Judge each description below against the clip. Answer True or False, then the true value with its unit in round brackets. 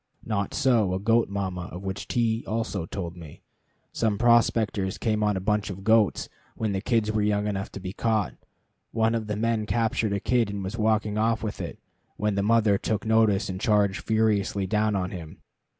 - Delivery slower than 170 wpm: False (200 wpm)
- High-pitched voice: False (105 Hz)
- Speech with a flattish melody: True (2.3 semitones)